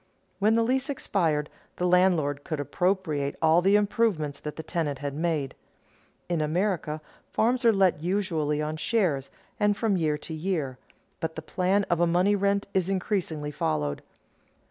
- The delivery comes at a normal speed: Yes, average, 160 wpm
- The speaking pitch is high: No, medium, 175 Hz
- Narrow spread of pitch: No, average, 4.7 semitones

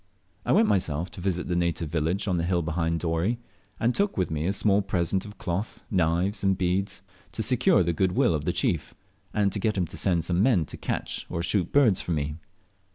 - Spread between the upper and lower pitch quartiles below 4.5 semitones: Yes, average, 3.0 semitones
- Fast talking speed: Yes, fast, 220 wpm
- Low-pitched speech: Yes, very low, 90 Hz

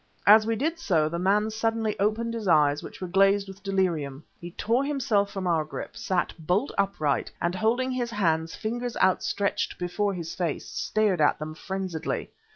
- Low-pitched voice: No, high, 195 Hz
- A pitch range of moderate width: Yes, average, 4.2 semitones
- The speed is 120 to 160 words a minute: No, average, 175 wpm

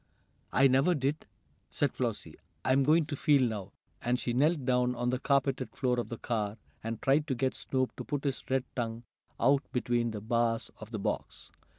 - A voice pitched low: Yes, low, 130 Hz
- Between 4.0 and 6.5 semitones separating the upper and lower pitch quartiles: No, average, 2.7 semitones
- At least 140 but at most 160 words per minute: No, average, 195 wpm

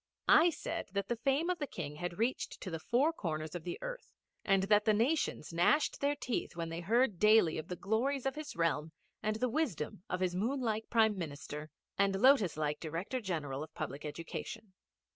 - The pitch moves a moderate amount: No, wide, 7.5 semitones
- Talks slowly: No, average, 200 wpm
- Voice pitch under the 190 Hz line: No, high, 200 Hz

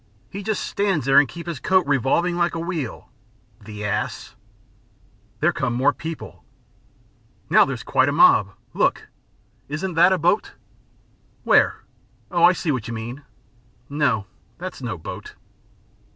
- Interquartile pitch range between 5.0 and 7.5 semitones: Yes, wide, 5.5 semitones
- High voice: No, medium, 160 Hz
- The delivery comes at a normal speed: Yes, average, 145 wpm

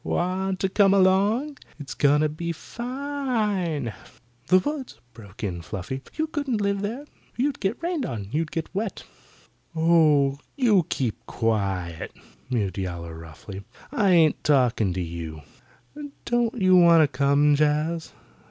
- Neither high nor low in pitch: Yes, medium, 160 Hz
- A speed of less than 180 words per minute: Yes, average, 140 wpm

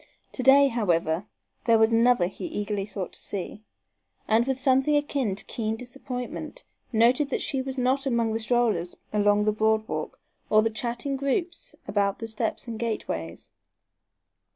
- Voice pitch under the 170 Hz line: No, high, 230 Hz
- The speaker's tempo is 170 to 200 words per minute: No, average, 160 wpm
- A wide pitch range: No, average, 3.7 semitones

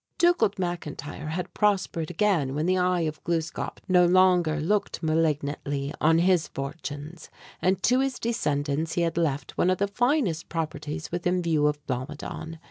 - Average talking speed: Yes, average, 155 wpm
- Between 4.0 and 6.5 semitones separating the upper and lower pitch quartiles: No, average, 3.5 semitones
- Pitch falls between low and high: Yes, medium, 165 Hz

